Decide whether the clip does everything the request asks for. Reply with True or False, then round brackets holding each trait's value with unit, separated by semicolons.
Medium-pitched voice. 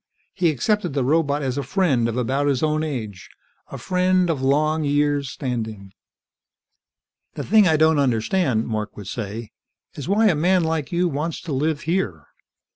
True (145 Hz)